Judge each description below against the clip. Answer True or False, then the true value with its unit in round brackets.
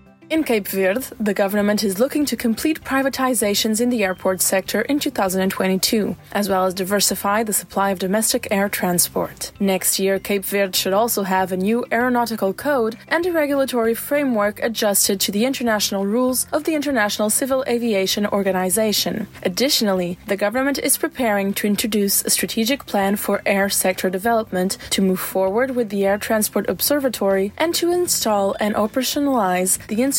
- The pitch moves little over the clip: False (4.0 semitones)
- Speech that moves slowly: False (160 wpm)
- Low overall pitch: False (210 Hz)